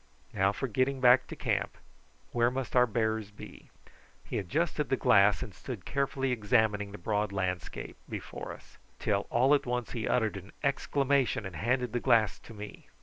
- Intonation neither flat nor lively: Yes, average, 3.9 semitones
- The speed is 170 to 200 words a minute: Yes, average, 175 wpm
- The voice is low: Yes, low, 120 Hz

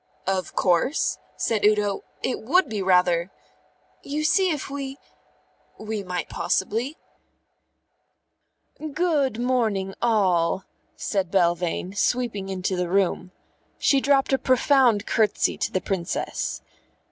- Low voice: No, high, 210 Hz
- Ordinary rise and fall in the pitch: No, wide, 6.1 semitones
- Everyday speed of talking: No, slow, 125 wpm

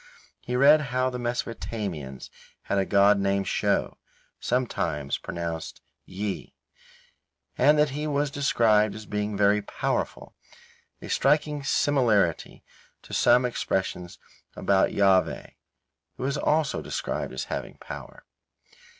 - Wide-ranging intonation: Yes, wide, 5.7 semitones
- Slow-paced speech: Yes, slow, 115 wpm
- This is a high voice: No, low, 110 Hz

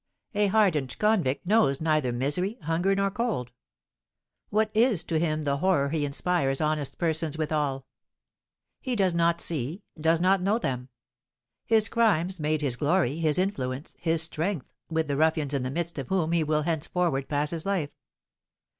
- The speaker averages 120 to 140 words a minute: No, average, 165 wpm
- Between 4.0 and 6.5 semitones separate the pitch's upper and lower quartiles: Yes, average, 4.5 semitones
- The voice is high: No, medium, 160 Hz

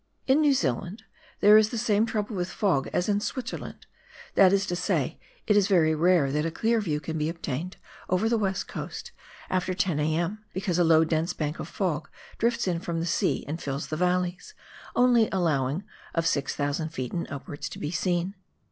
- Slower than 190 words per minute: No, average, 195 wpm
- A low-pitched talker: No, medium, 180 Hz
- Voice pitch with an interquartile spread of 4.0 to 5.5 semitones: Yes, average, 4.5 semitones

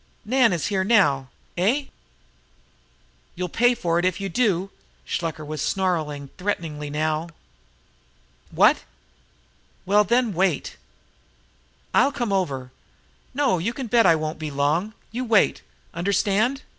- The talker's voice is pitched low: No, medium, 185 Hz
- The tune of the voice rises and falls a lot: Yes, wide, 6.1 semitones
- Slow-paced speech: Yes, slow, 110 wpm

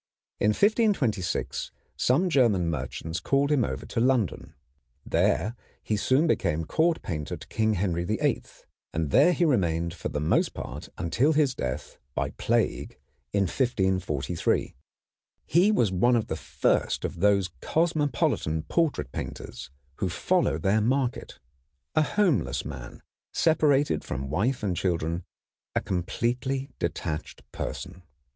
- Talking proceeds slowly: Yes, slow, 130 wpm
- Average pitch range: No, wide, 8.6 semitones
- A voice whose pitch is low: Yes, low, 110 Hz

